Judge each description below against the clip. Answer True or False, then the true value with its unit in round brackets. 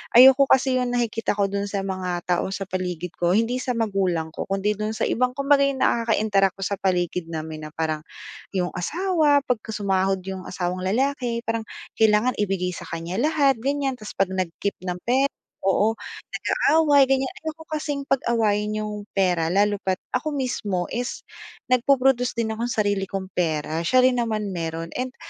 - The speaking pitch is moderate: False (210 Hz)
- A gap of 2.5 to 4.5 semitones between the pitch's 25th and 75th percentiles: False (5.3 semitones)